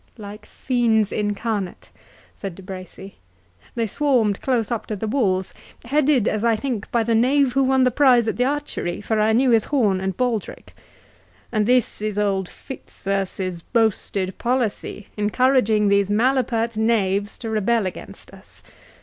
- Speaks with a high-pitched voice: Yes, high, 220 Hz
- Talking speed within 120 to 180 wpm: Yes, average, 155 wpm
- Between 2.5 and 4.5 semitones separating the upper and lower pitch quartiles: Yes, average, 3.6 semitones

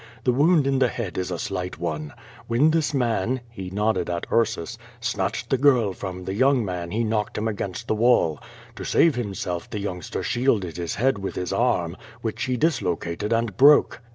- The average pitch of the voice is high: No, low, 110 Hz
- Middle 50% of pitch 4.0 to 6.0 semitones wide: Yes, average, 5.3 semitones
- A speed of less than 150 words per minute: No, average, 195 wpm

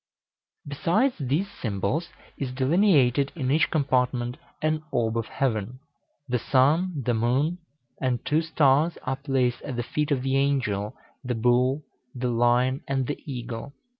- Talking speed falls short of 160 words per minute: Yes, average, 145 wpm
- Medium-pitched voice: No, low, 130 Hz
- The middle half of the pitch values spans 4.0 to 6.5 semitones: No, average, 3.2 semitones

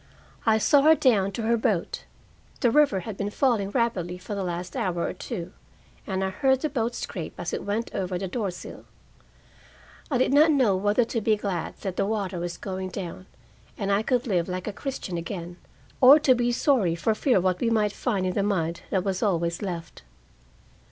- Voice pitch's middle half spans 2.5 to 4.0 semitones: No, average, 4.4 semitones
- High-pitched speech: Yes, high, 200 Hz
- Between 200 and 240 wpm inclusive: Yes, fast, 205 wpm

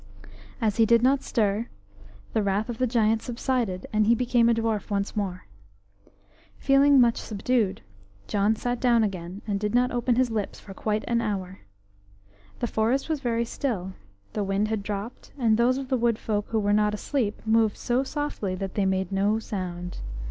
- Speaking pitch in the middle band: No, high, 220 Hz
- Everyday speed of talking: Yes, average, 185 wpm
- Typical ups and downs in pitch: Yes, average, 3.1 semitones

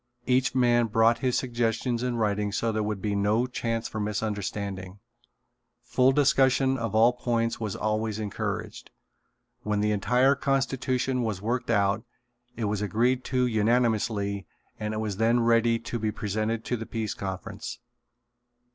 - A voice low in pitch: Yes, low, 115 Hz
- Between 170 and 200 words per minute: No, average, 150 wpm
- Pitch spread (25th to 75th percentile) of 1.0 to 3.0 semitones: Yes, average, 2.7 semitones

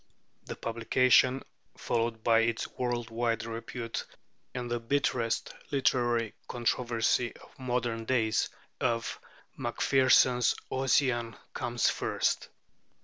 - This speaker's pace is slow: Yes, slow, 95 wpm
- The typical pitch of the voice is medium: No, low, 120 Hz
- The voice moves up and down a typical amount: No, narrow, 1.6 semitones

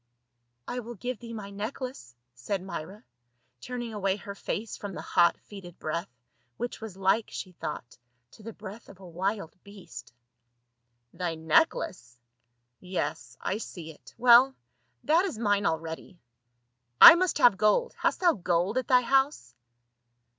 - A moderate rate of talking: Yes, average, 150 wpm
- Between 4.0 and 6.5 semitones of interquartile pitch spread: Yes, wide, 5.5 semitones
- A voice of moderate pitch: No, high, 200 Hz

